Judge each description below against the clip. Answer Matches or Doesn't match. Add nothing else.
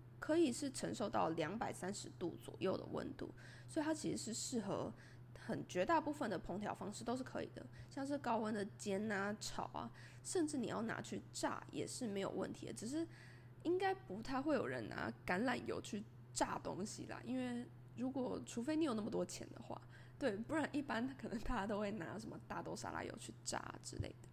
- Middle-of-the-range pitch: Doesn't match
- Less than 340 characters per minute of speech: Matches